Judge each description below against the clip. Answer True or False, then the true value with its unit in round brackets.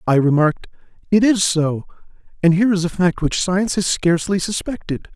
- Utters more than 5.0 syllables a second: True (5.8 syllables/s)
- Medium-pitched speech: True (180 Hz)